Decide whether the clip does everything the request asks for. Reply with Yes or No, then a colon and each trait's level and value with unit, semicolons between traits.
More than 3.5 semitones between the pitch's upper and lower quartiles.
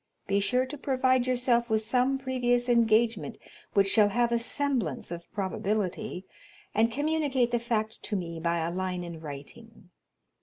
Yes: average, 4.8 semitones